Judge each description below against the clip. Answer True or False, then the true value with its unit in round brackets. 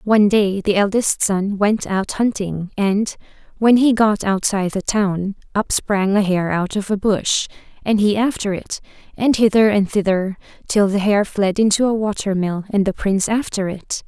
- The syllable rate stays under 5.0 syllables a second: True (4.6 syllables/s)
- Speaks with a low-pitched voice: False (205 Hz)